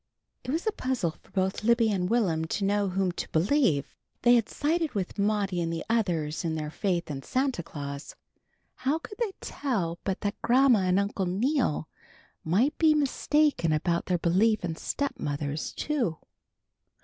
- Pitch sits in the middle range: No, high, 200 Hz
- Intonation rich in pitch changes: Yes, wide, 7.3 semitones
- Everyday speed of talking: Yes, average, 165 wpm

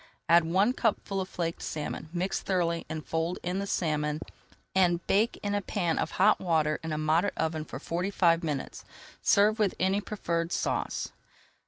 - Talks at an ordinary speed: Yes, average, 175 wpm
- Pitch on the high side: No, medium, 175 Hz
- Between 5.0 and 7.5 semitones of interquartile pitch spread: No, average, 3.3 semitones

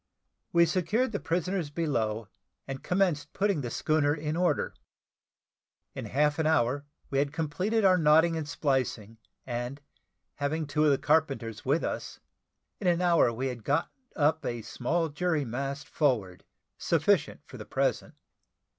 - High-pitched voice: No, medium, 150 Hz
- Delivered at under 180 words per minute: Yes, average, 150 wpm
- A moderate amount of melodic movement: Yes, average, 4.0 semitones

